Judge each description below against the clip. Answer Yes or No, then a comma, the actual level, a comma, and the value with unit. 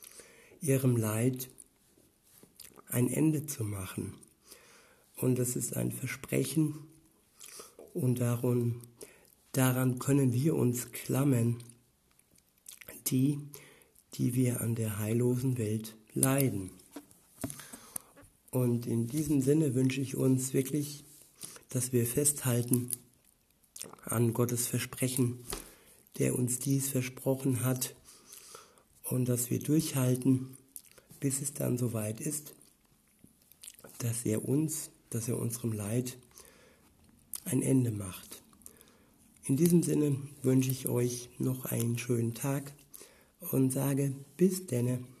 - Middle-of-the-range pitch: No, low, 130 Hz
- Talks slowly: Yes, slow, 105 wpm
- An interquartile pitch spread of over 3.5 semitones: No, narrow, 2.4 semitones